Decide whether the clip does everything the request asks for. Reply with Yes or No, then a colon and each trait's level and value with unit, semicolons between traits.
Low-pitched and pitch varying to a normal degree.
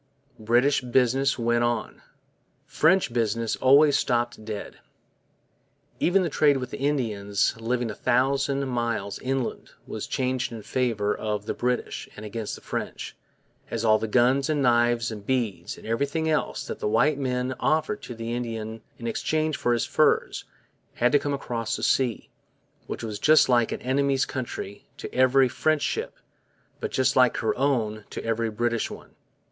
Yes: low, 120 Hz; average, 3.1 semitones